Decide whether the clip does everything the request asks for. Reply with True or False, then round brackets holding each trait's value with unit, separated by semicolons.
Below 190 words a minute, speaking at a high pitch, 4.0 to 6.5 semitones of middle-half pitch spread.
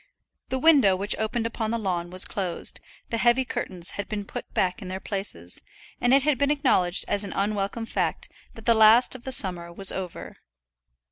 False (195 wpm; 210 Hz; 4.3 semitones)